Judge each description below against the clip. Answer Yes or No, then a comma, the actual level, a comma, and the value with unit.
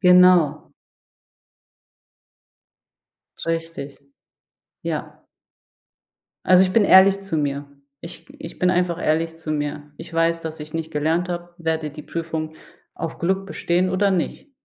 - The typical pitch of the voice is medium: Yes, medium, 165 Hz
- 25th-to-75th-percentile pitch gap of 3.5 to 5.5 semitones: No, narrow, 2.5 semitones